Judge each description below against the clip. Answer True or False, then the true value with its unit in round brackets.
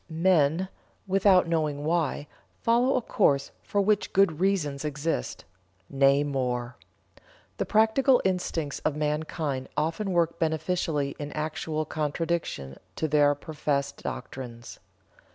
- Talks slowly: True (115 wpm)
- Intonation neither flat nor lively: True (4.0 semitones)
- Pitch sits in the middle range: True (155 Hz)